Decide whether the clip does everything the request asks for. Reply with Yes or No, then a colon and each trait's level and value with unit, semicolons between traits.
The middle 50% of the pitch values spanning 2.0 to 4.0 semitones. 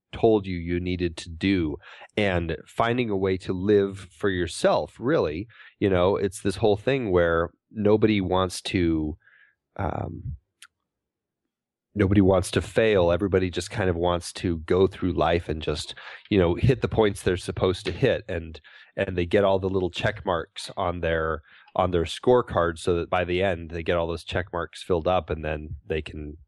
Yes: average, 2.8 semitones